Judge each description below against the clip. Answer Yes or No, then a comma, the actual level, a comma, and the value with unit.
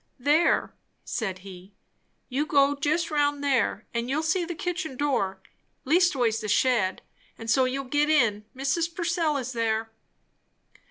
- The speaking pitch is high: Yes, very high, 275 Hz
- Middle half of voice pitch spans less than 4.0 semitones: No, wide, 5.4 semitones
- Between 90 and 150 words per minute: Yes, average, 145 wpm